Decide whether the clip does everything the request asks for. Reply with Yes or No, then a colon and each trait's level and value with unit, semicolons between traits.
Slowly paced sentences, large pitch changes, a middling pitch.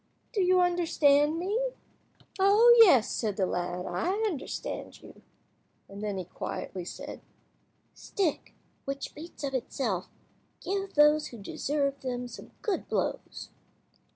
No: slow, 125 wpm; wide, 8.7 semitones; very high, 290 Hz